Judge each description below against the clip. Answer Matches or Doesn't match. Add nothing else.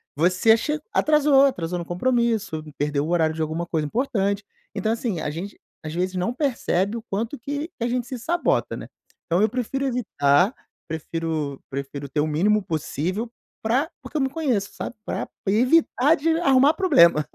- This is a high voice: Matches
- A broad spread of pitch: Matches